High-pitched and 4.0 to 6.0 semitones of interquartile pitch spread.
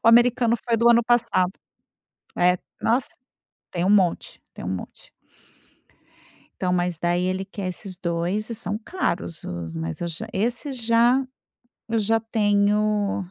Yes: high, 205 Hz; average, 4.4 semitones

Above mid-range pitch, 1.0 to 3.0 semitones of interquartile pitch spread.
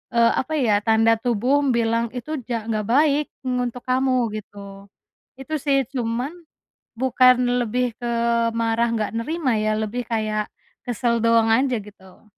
Yes: high, 235 Hz; narrow, 2.5 semitones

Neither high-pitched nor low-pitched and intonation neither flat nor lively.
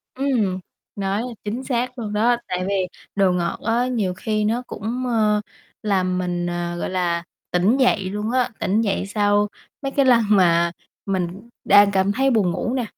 No: high, 205 Hz; average, 4.3 semitones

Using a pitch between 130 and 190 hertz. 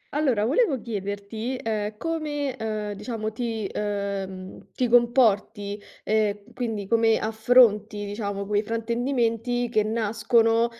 No: high, 220 Hz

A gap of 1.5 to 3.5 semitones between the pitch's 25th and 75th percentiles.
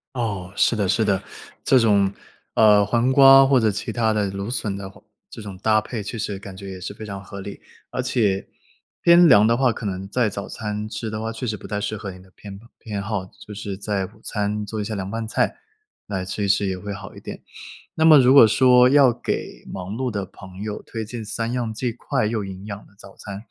Yes: average, 2.8 semitones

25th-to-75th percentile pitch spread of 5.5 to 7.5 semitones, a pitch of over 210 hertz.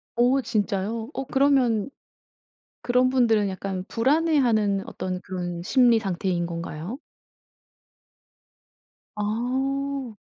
No: average, 5.1 semitones; high, 225 Hz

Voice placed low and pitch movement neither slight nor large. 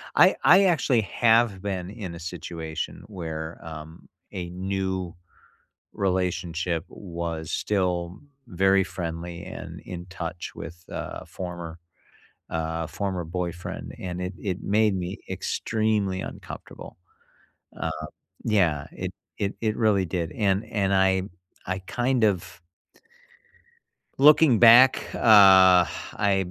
Yes: very low, 95 Hz; average, 3.0 semitones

